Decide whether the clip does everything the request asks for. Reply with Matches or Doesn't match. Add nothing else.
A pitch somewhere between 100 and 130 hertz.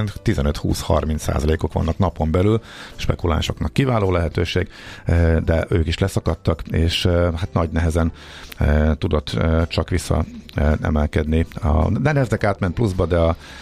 Doesn't match